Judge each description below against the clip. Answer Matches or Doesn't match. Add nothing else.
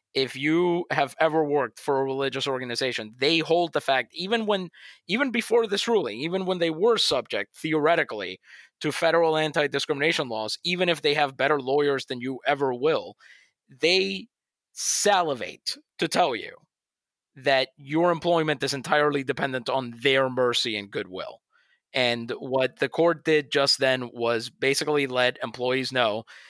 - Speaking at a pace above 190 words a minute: Doesn't match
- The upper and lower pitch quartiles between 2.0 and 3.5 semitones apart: Doesn't match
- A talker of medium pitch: Matches